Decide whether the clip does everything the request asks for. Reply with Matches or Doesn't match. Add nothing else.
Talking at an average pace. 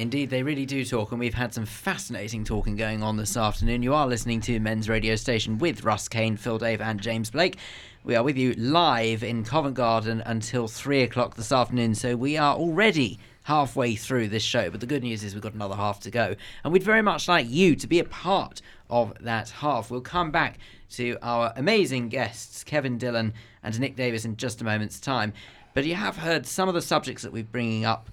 Doesn't match